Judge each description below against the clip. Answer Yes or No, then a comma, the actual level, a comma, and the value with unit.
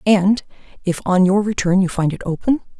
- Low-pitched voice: No, high, 190 Hz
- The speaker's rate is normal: Yes, average, 195 wpm